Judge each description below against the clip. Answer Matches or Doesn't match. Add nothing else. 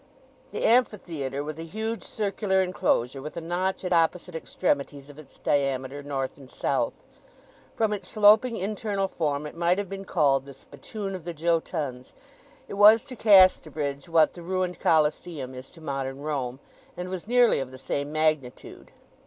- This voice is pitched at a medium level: Matches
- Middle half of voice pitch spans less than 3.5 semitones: Doesn't match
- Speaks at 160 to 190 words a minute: Matches